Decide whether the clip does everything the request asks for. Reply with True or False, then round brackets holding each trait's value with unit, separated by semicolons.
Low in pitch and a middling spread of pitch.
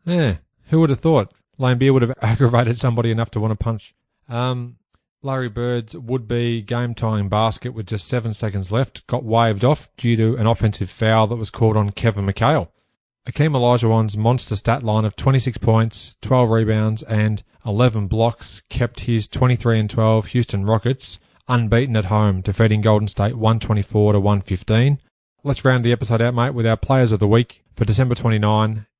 False (115 Hz; 2.3 semitones)